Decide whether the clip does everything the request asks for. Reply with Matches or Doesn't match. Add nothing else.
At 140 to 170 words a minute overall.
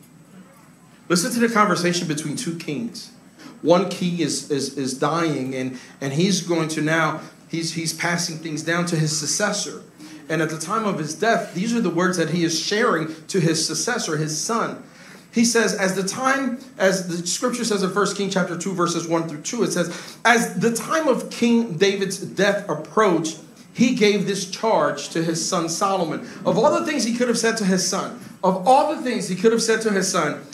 Doesn't match